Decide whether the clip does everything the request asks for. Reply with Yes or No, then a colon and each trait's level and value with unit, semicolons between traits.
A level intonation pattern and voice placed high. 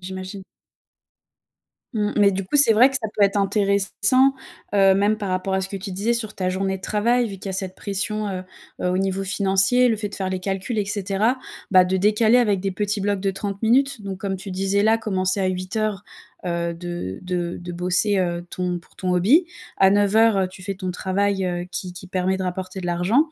Yes: narrow, 2.1 semitones; high, 195 Hz